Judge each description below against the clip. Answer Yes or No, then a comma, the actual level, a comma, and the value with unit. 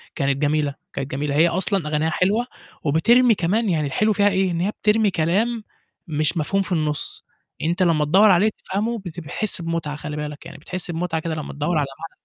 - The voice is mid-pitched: Yes, medium, 170 Hz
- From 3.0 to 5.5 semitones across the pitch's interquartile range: Yes, average, 4.6 semitones